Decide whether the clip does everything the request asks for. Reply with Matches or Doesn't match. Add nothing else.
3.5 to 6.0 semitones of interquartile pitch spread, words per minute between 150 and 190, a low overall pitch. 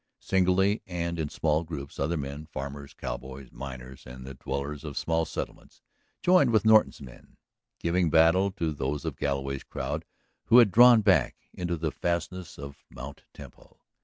Matches